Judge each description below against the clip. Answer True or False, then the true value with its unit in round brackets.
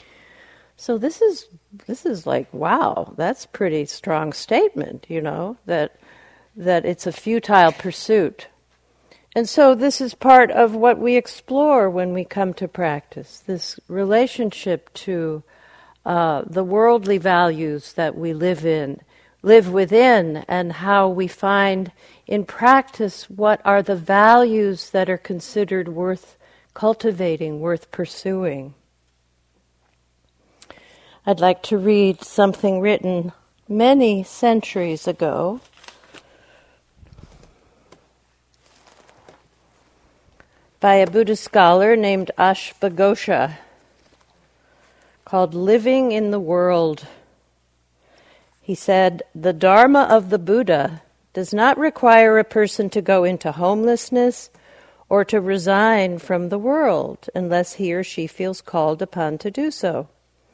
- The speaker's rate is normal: False (115 wpm)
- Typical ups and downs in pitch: True (4.3 semitones)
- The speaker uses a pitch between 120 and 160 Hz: False (190 Hz)